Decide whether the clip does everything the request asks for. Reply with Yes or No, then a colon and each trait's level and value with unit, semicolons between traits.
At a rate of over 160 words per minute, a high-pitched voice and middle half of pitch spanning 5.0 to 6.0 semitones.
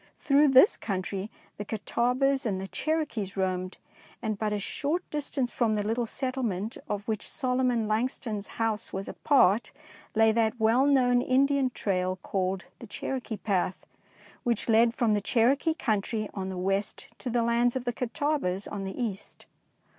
No: average, 170 wpm; high, 225 Hz; average, 4.1 semitones